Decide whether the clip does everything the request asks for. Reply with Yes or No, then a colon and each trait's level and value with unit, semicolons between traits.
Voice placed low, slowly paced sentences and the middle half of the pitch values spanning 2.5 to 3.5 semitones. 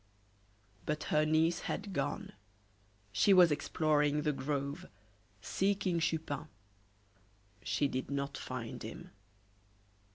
No: medium, 150 Hz; slow, 100 wpm; average, 2.9 semitones